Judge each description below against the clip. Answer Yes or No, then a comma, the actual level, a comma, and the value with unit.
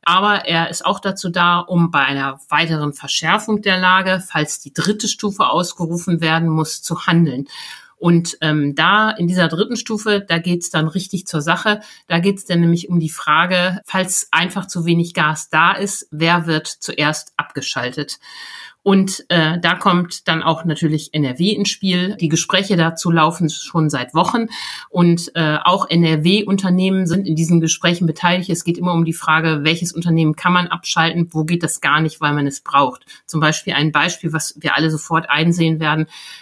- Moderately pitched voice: Yes, medium, 170 Hz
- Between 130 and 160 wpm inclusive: No, average, 185 wpm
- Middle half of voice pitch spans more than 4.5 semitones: No, narrow, 2.6 semitones